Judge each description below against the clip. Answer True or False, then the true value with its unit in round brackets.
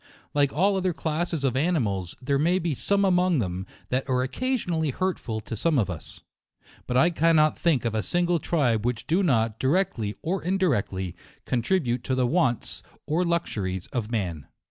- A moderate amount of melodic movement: False (7.3 semitones)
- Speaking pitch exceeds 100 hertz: True (140 Hz)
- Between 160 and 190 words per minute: True (170 wpm)